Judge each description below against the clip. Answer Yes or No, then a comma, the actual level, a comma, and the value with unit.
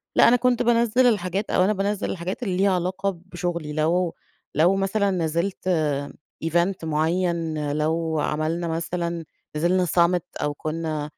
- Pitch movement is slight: No, average, 3.2 semitones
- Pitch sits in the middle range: Yes, medium, 175 Hz